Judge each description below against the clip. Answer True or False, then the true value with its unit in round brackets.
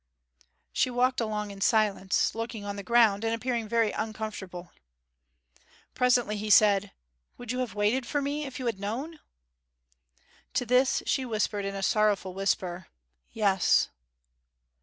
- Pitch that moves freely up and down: False (3.4 semitones)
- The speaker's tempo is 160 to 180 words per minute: False (140 wpm)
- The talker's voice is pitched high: True (215 Hz)